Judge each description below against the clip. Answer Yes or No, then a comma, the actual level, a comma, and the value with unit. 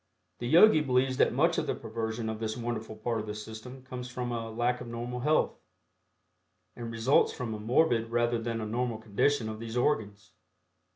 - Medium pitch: No, low, 115 Hz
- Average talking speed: Yes, average, 190 wpm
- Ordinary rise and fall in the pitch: No, narrow, 2.0 semitones